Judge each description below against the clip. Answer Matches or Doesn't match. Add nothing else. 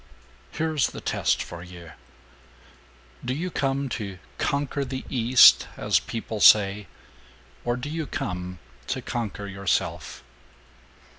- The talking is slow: Matches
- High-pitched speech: Doesn't match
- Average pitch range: Doesn't match